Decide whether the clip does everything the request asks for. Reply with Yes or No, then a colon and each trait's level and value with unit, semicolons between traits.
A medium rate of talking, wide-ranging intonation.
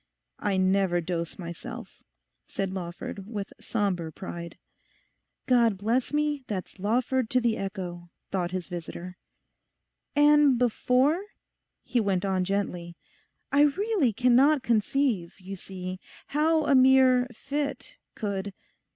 No: slow, 115 wpm; wide, 6.0 semitones